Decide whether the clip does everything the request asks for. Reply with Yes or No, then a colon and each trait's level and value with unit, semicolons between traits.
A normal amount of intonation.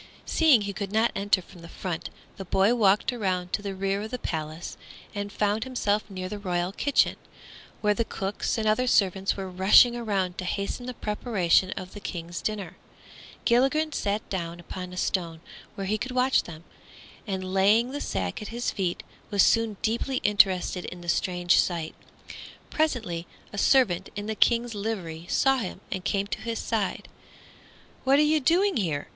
Yes: average, 4.0 semitones